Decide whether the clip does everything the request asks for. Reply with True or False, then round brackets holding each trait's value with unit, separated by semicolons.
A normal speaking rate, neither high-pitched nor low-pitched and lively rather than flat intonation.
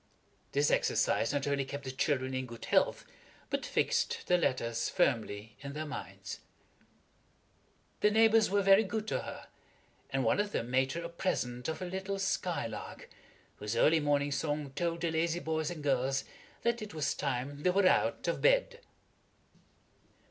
True (165 wpm; 150 Hz; 5.8 semitones)